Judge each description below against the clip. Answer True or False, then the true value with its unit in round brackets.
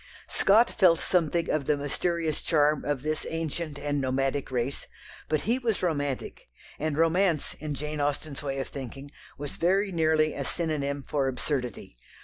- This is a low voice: False (150 Hz)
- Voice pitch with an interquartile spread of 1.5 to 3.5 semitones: True (2.8 semitones)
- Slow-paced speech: False (155 wpm)